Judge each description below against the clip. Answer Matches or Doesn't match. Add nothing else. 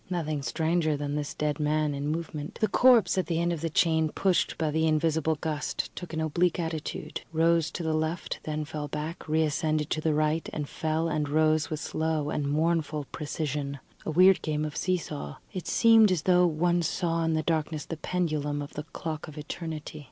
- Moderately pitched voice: Matches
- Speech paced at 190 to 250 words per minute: Matches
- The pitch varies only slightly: Matches